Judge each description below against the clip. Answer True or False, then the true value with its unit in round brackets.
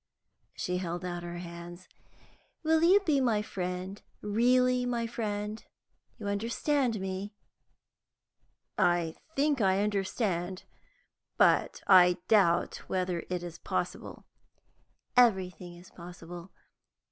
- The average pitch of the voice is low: False (190 Hz)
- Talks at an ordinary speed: False (105 wpm)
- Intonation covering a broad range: False (4.6 semitones)